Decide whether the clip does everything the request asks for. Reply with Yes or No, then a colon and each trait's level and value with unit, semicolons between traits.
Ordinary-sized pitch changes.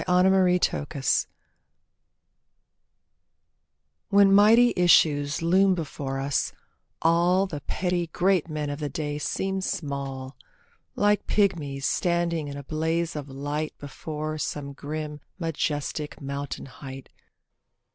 Yes: average, 3.9 semitones